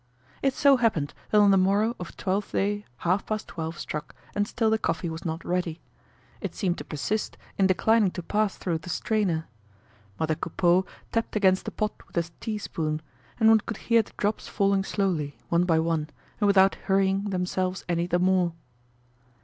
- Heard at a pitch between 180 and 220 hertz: Yes, high, 190 Hz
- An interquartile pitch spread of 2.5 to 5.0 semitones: Yes, average, 3.6 semitones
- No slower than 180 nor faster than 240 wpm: Yes, average, 185 wpm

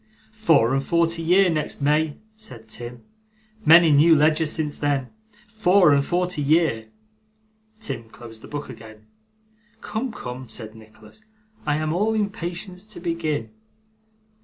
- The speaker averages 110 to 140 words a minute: Yes, slow, 135 wpm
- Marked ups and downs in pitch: Yes, wide, 6.1 semitones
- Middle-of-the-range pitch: Yes, medium, 155 Hz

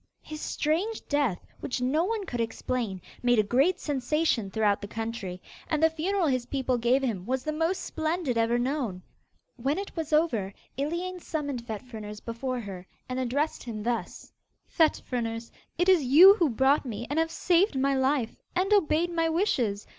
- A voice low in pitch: No, very high, 265 Hz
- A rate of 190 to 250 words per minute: No, average, 175 wpm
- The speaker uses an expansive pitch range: Yes, wide, 5.7 semitones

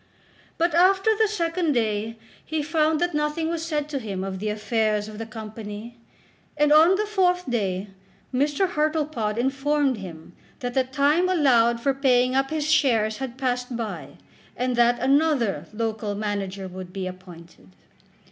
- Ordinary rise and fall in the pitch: No, wide, 6.3 semitones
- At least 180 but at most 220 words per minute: No, average, 155 wpm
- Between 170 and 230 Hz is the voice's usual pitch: No, very high, 250 Hz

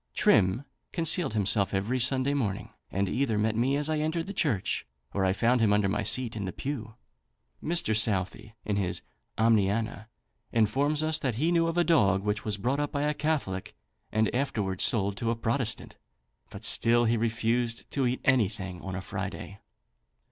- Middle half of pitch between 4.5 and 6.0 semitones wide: Yes, wide, 5.5 semitones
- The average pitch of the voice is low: Yes, low, 115 Hz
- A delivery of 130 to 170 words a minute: No, average, 180 wpm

